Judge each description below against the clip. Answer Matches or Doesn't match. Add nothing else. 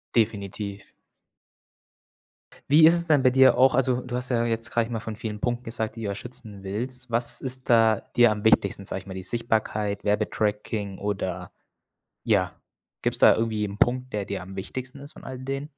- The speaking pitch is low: Matches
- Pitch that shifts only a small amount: Doesn't match